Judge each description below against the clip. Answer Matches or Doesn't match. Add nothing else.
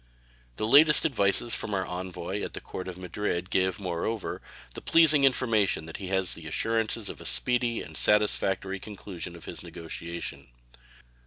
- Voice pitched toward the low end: Matches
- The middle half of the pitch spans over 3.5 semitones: Matches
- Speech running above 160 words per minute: Doesn't match